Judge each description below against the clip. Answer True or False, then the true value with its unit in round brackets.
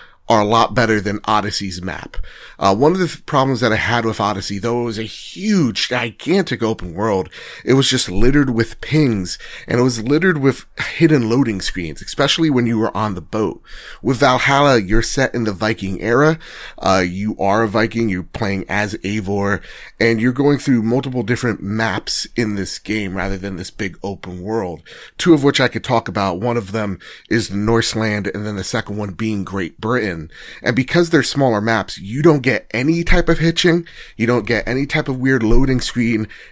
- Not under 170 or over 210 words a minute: True (200 wpm)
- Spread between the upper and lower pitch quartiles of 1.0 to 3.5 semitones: False (4.3 semitones)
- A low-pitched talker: True (115 Hz)